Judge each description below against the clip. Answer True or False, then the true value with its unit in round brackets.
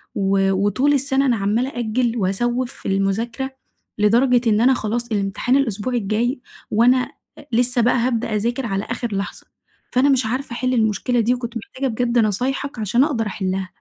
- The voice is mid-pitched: False (235 Hz)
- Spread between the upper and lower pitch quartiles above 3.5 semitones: False (3.2 semitones)